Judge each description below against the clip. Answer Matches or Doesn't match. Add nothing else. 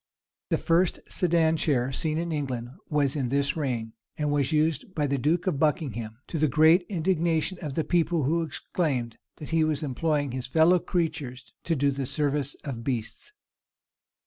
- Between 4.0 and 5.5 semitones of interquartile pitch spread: Doesn't match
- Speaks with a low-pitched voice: Doesn't match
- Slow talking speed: Doesn't match